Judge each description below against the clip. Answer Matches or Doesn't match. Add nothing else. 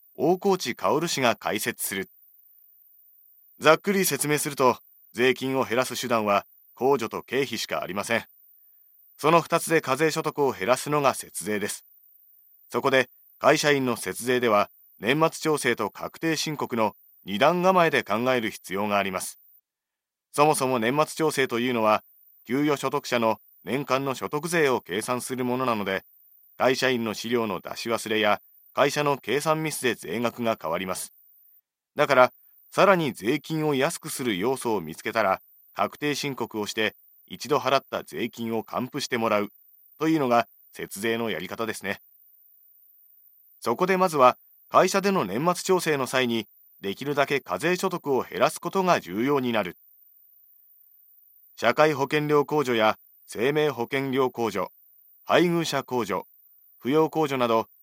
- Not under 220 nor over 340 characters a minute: Matches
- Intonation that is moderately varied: Matches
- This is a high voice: Doesn't match